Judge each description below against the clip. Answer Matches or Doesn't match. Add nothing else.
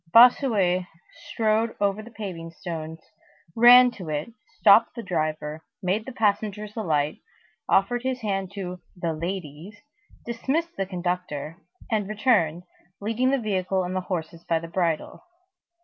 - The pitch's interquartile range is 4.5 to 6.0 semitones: Matches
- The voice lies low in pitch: Doesn't match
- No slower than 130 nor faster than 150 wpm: Matches